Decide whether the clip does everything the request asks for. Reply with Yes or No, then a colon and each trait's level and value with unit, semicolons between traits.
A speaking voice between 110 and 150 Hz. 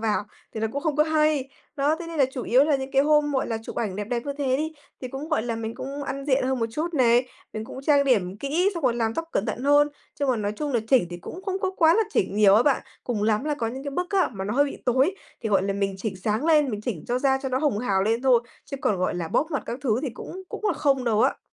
No: very high, 260 Hz